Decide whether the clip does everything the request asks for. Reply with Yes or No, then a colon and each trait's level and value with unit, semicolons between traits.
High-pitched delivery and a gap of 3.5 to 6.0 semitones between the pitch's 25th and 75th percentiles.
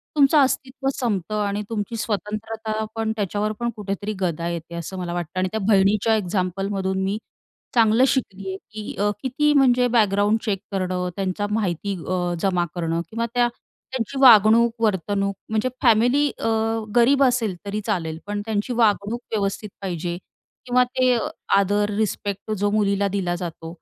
No: high, 205 Hz; average, 3.0 semitones